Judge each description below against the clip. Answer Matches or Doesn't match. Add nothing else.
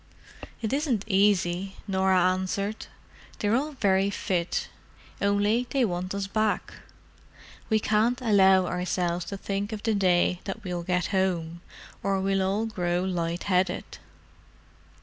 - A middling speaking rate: Doesn't match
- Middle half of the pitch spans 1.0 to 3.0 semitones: Matches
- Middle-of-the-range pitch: Doesn't match